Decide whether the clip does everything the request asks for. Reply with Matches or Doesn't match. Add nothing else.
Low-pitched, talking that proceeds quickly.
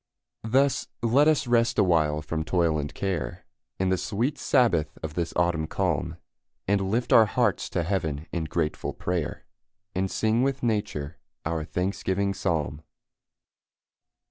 Doesn't match